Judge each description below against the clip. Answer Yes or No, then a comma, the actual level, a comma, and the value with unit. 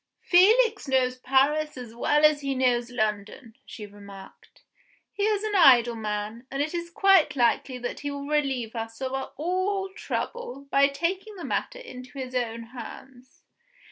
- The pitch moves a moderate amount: No, wide, 6.0 semitones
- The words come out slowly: No, average, 160 wpm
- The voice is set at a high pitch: Yes, very high, 270 Hz